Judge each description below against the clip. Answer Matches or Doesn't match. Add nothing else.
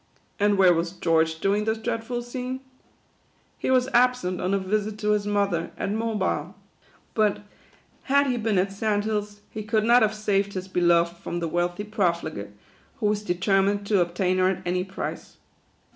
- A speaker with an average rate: Matches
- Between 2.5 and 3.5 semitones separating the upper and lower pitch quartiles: Matches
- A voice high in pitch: Matches